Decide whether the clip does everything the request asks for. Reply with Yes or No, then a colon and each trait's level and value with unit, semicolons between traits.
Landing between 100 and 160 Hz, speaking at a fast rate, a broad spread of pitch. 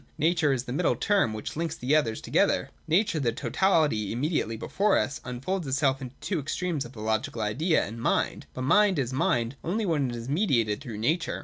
Yes: medium, 140 Hz; fast, 210 wpm; wide, 5.9 semitones